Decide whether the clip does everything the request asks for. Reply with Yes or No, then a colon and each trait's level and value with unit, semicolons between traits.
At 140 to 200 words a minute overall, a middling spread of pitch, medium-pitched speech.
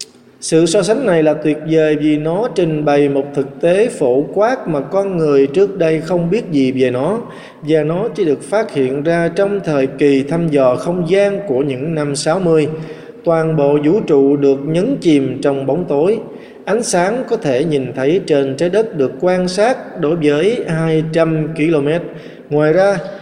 Yes: average, 185 wpm; average, 3.6 semitones; medium, 155 Hz